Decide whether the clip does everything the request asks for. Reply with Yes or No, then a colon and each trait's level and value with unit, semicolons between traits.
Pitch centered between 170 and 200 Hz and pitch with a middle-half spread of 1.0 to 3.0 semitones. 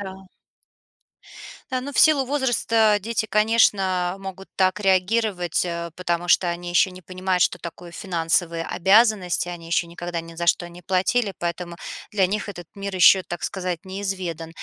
Yes: medium, 185 Hz; average, 2.7 semitones